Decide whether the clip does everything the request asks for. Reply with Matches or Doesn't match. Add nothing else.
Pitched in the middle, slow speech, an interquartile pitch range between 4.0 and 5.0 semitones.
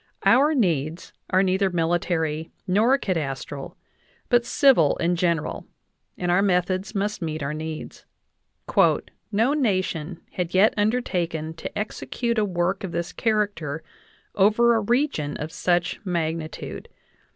Matches